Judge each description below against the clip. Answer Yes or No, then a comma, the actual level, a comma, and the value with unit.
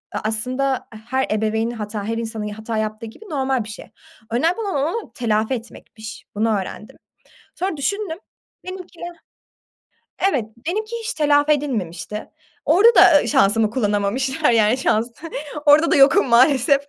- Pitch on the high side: Yes, very high, 250 Hz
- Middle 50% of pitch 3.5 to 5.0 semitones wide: No, wide, 5.4 semitones